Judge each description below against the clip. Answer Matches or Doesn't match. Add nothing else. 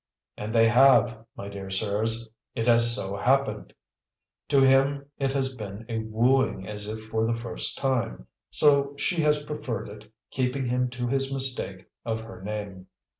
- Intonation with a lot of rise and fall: Doesn't match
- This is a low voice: Matches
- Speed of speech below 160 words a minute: Doesn't match